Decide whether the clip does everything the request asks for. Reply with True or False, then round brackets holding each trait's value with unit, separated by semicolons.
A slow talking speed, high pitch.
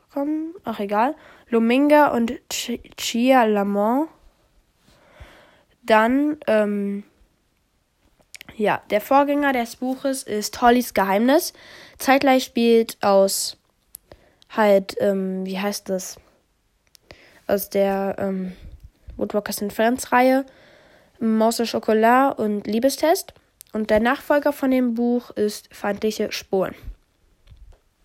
True (100 wpm; 230 Hz)